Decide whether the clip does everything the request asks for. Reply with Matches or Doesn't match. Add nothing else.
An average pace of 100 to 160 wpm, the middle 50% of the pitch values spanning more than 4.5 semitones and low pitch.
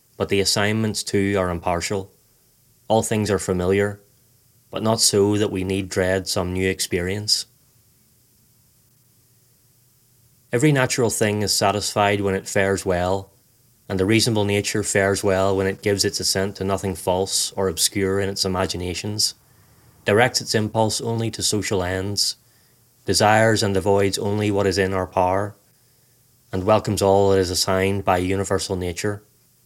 Doesn't match